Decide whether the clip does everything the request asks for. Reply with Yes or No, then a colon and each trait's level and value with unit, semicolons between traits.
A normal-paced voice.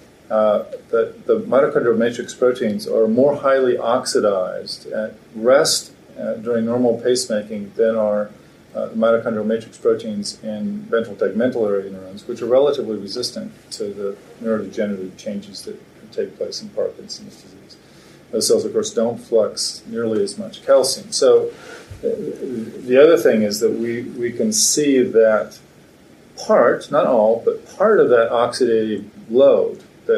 Yes: average, 145 wpm